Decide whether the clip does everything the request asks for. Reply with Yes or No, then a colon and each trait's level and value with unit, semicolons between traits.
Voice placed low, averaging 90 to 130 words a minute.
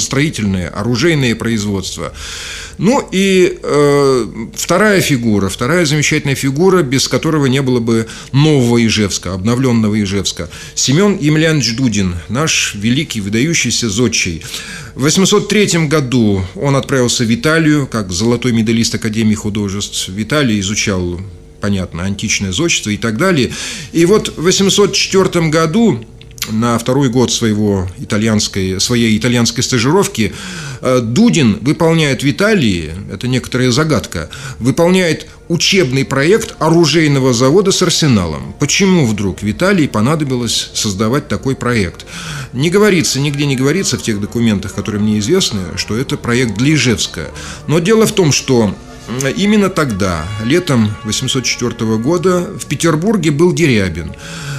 Yes: low, 125 Hz; average, 125 wpm